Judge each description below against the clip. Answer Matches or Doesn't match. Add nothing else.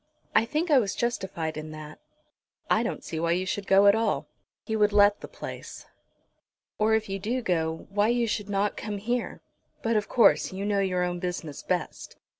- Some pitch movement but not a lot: Matches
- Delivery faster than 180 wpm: Matches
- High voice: Matches